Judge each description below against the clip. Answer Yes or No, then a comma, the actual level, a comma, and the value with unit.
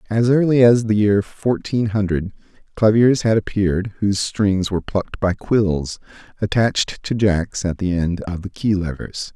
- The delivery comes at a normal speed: Yes, average, 165 wpm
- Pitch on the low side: Yes, low, 105 Hz